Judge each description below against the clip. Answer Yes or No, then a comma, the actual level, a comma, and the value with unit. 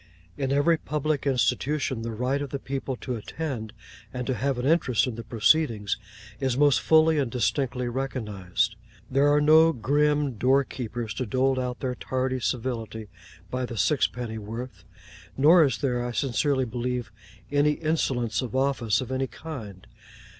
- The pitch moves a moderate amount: Yes, average, 3.3 semitones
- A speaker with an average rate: Yes, average, 160 wpm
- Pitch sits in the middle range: No, low, 130 Hz